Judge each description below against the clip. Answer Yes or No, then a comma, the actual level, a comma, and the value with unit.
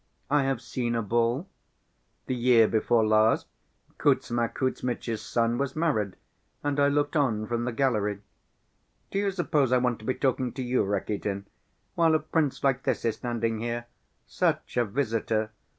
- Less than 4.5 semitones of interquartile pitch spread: Yes, average, 3.5 semitones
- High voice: No, low, 120 Hz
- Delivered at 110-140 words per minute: No, average, 165 wpm